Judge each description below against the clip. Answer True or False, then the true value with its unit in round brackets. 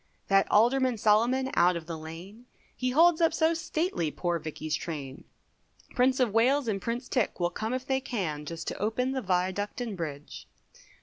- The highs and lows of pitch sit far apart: True (7.0 semitones)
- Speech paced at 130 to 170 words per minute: False (180 wpm)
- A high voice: True (215 Hz)